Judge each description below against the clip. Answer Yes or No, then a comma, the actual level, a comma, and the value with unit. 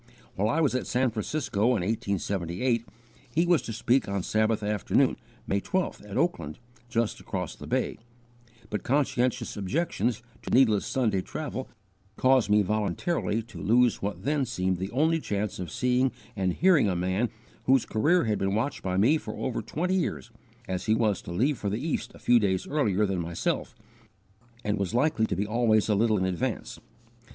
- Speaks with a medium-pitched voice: No, low, 110 Hz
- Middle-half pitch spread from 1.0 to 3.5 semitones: No, average, 4.8 semitones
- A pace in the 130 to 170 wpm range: No, average, 180 wpm